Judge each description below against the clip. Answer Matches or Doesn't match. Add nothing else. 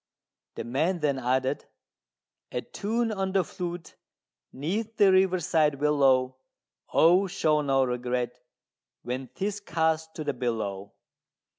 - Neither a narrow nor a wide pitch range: Doesn't match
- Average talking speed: Doesn't match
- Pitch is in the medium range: Matches